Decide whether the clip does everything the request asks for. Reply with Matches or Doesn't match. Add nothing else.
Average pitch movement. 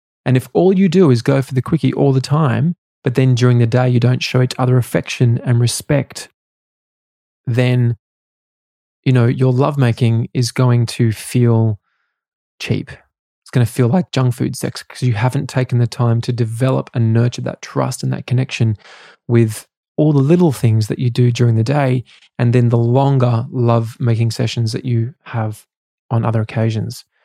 Doesn't match